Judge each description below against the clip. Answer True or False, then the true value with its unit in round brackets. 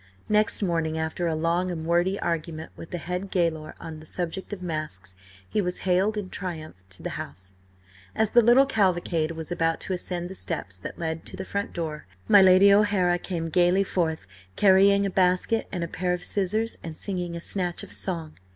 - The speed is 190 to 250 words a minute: True (195 wpm)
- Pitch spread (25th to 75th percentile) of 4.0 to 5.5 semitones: False (2.9 semitones)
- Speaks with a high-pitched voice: False (175 Hz)